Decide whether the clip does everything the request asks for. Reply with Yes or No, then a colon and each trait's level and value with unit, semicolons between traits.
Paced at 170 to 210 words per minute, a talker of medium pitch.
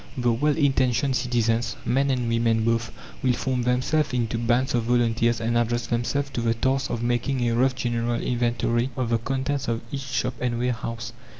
No: average, 185 wpm; low, 120 Hz